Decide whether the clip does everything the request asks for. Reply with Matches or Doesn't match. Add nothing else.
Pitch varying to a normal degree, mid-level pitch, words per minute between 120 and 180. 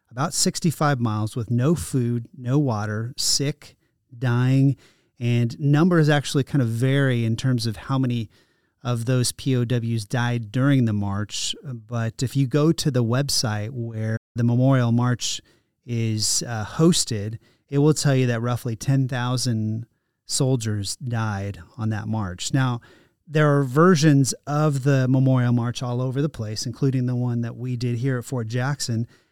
Doesn't match